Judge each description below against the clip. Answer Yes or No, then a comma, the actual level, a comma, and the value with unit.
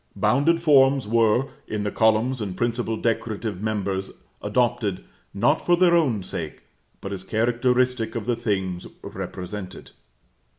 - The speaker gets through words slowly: Yes, slow, 130 wpm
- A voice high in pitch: No, low, 110 Hz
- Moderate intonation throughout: Yes, average, 3.8 semitones